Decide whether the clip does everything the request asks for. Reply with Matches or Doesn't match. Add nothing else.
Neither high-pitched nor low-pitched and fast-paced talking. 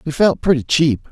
Matches